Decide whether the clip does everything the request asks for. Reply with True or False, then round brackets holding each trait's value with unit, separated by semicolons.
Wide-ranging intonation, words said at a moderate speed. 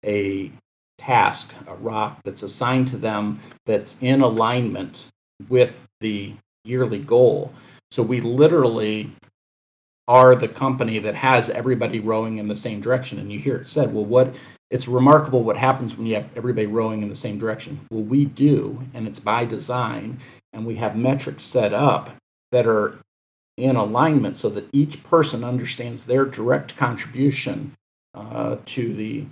False (3.2 semitones; 160 wpm)